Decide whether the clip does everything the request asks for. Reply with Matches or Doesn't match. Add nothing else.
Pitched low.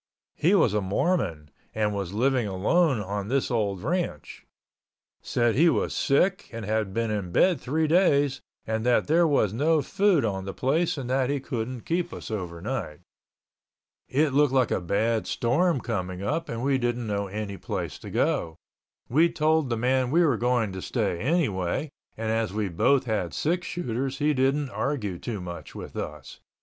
Matches